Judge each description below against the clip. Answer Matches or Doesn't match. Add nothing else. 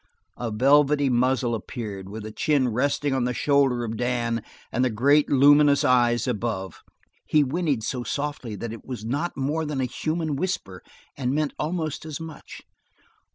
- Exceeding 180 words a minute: Doesn't match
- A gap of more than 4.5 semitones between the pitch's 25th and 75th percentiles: Doesn't match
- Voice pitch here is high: Doesn't match